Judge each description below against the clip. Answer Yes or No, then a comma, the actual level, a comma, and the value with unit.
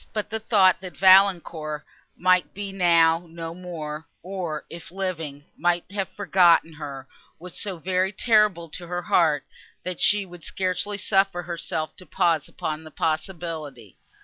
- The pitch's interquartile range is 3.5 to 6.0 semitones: No, average, 2.9 semitones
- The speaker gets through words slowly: No, average, 150 wpm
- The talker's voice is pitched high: No, medium, 175 Hz